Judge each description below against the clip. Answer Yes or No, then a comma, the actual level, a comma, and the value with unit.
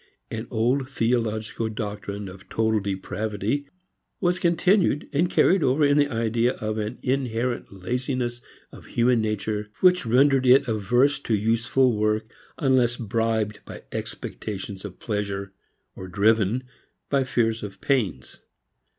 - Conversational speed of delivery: No, slow, 130 wpm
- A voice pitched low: Yes, low, 115 Hz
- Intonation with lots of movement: No, average, 3.6 semitones